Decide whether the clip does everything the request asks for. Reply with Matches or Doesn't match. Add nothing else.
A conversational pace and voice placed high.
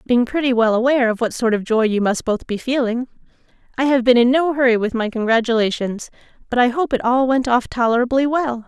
Doesn't match